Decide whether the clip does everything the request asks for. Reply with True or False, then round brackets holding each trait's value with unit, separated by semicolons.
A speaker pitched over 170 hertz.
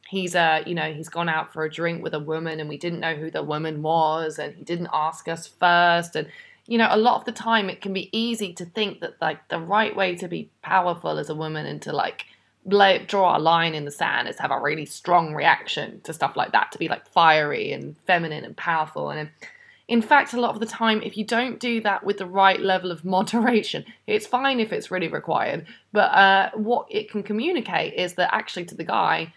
True (185 Hz)